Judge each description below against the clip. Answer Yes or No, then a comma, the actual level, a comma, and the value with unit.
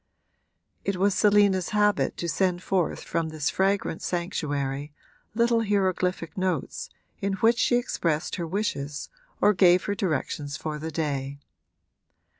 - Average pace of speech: No, slow, 130 wpm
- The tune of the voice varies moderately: Yes, average, 4.5 semitones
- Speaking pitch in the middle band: Yes, medium, 180 Hz